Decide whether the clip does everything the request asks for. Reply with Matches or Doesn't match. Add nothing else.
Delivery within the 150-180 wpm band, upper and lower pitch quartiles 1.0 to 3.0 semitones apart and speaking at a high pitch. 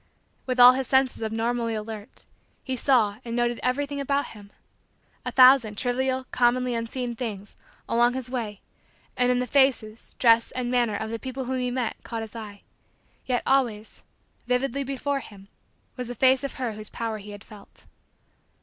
Matches